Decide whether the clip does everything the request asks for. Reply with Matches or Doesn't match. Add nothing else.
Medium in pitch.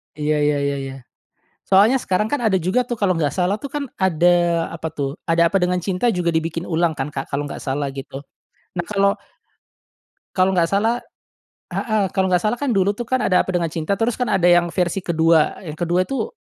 Matches